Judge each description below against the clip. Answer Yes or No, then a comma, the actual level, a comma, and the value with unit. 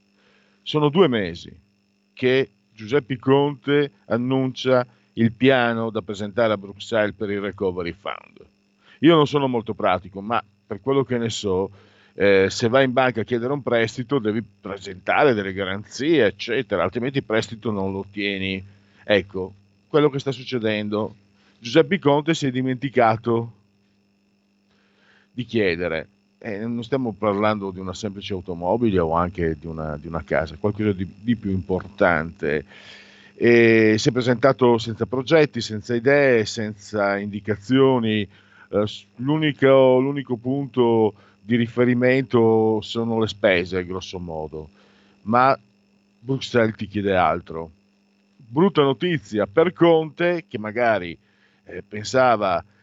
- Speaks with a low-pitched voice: Yes, low, 110 Hz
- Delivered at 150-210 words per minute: No, average, 130 wpm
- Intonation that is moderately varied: Yes, average, 4.1 semitones